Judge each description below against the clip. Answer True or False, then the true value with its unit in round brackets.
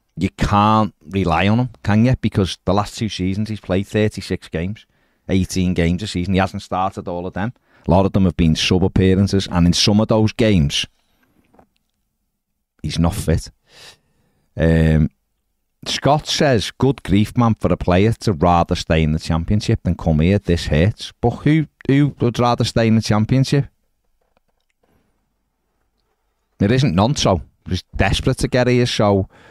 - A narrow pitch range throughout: False (4.0 semitones)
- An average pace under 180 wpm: True (165 wpm)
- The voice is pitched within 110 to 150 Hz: False (95 Hz)